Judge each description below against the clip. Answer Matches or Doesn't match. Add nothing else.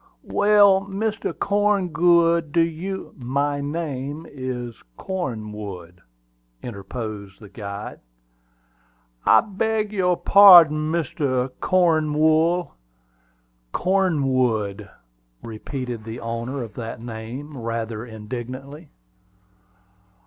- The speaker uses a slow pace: Matches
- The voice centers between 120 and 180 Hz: Matches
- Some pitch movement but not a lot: Doesn't match